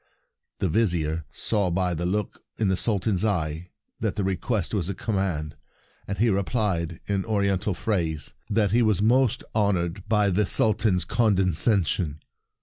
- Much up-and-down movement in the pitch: No, average, 3.5 semitones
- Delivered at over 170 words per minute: No, average, 150 wpm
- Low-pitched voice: Yes, low, 100 Hz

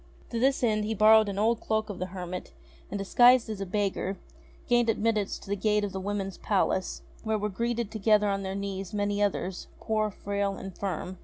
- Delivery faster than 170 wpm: Yes, average, 200 wpm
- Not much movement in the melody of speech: Yes, narrow, 2.0 semitones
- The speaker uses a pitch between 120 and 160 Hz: No, high, 205 Hz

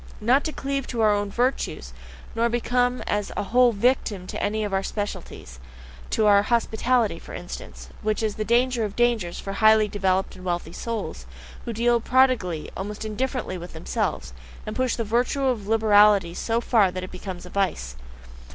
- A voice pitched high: Yes, high, 215 Hz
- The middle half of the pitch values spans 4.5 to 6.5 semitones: No, average, 3.6 semitones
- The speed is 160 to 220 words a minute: Yes, average, 180 wpm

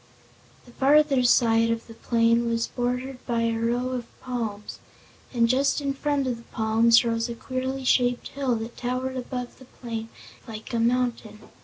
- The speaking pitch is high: Yes, high, 240 Hz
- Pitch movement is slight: Yes, narrow, 1.9 semitones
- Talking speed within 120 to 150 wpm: No, average, 170 wpm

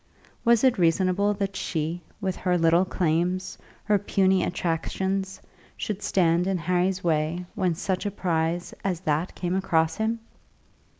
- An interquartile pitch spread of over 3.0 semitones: No, narrow, 2.4 semitones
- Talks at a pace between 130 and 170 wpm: Yes, average, 140 wpm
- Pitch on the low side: No, medium, 180 Hz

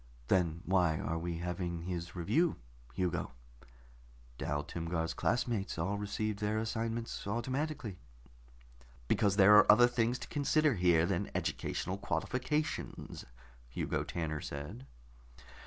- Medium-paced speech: No, slow, 115 wpm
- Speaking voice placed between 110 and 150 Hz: No, very low, 95 Hz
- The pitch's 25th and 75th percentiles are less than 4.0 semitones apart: No, average, 5.3 semitones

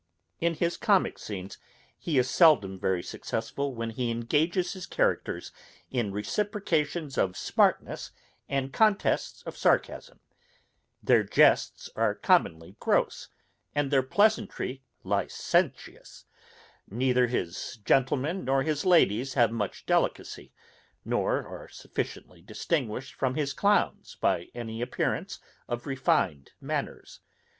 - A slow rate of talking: Yes, slow, 115 wpm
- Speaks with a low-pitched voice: Yes, low, 130 Hz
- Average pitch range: No, wide, 5.9 semitones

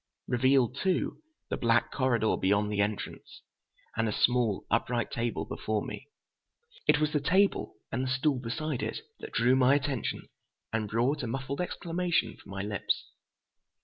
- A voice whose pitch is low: Yes, low, 125 Hz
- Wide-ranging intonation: No, average, 3.8 semitones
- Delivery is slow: No, average, 155 wpm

